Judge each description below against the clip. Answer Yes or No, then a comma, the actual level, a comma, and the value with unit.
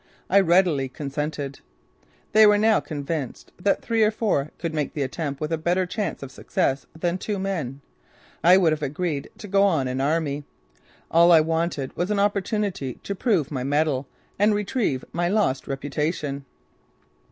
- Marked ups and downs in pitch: Yes, wide, 5.7 semitones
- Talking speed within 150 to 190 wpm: Yes, average, 165 wpm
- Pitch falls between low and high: Yes, medium, 165 Hz